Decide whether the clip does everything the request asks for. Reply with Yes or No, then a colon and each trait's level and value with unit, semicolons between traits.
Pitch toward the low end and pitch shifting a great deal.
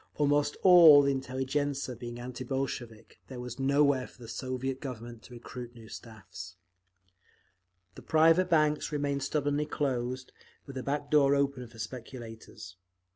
No: low, 130 Hz; average, 3.0 semitones